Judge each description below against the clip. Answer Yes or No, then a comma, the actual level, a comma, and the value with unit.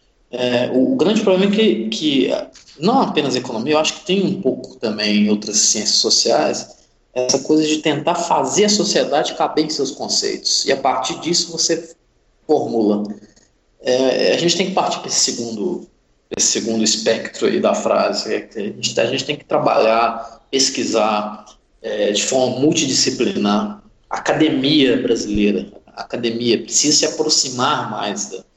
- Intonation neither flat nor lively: No, wide, 7.1 semitones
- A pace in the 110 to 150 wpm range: No, average, 160 wpm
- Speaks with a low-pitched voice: Yes, low, 130 Hz